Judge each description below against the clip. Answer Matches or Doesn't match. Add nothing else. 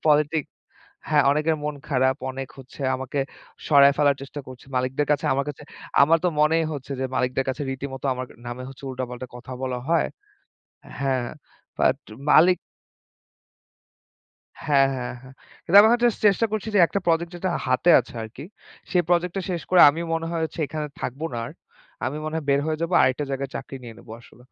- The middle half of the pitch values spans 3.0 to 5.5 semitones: Matches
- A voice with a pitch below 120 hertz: Doesn't match